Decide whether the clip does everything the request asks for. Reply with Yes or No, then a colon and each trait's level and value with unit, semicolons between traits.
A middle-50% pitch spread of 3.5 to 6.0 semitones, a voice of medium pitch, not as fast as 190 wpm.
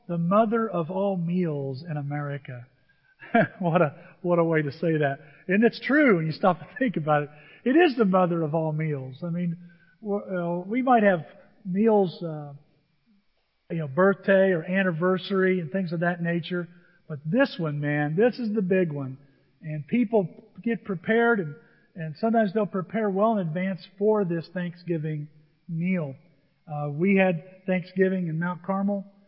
Yes: average, 4.1 semitones; medium, 180 Hz; average, 170 wpm